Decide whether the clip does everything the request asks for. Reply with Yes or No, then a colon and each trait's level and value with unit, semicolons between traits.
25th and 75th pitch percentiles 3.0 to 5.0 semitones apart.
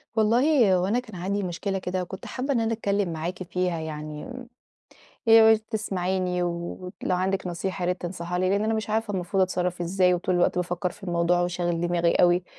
No: narrow, 2.5 semitones